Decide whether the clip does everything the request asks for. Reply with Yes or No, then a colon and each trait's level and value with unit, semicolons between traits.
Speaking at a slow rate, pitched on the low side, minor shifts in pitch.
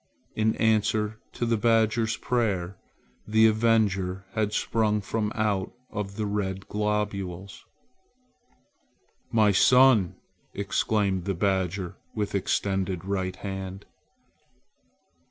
Yes: slow, 95 wpm; low, 105 Hz; narrow, 2.2 semitones